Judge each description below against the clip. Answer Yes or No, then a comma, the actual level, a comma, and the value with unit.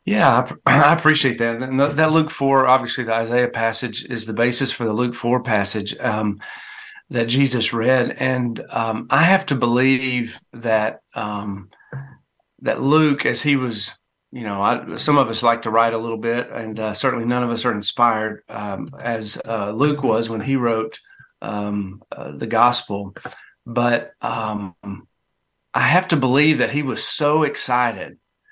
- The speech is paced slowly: No, average, 170 wpm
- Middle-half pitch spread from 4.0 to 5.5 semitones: No, average, 3.1 semitones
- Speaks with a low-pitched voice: Yes, low, 120 Hz